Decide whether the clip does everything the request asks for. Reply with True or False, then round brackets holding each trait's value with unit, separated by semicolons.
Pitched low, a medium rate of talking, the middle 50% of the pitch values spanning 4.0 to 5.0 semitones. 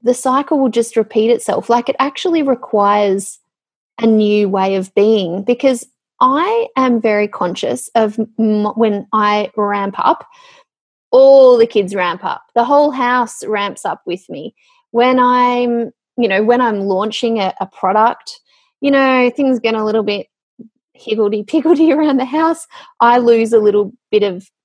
False (235 Hz; 160 wpm; 4.4 semitones)